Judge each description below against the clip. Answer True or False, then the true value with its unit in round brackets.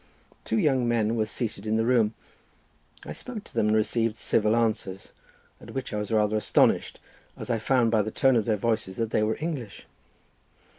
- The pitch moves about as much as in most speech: False (1.8 semitones)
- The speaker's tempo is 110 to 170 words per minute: False (195 wpm)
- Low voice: True (110 Hz)